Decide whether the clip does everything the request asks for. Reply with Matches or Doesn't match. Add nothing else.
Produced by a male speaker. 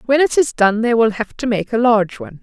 Doesn't match